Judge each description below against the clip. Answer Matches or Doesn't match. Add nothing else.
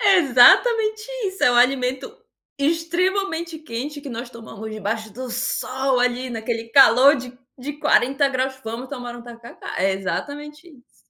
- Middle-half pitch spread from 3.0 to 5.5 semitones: Matches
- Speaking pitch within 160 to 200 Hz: Doesn't match